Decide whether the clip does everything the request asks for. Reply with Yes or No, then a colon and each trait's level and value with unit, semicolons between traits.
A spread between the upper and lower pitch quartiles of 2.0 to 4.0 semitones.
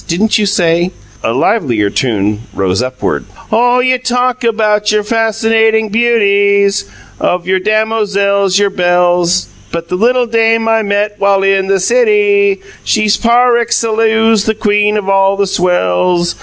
Yes: average, 3.7 semitones